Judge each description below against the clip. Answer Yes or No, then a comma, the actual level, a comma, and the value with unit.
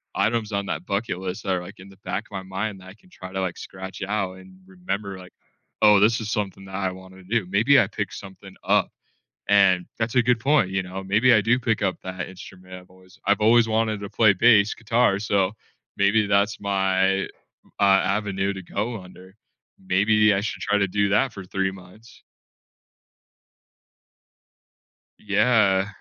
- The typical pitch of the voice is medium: No, low, 100 Hz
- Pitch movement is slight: Yes, narrow, 2.2 semitones